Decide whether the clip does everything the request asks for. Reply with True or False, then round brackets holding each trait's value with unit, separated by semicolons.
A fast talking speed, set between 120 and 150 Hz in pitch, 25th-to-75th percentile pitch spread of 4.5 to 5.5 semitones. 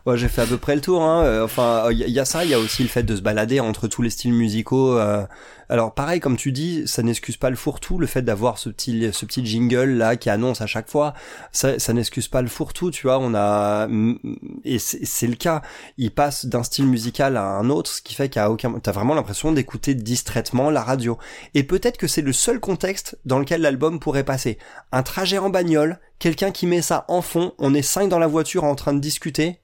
True (245 wpm; 130 Hz; 5.0 semitones)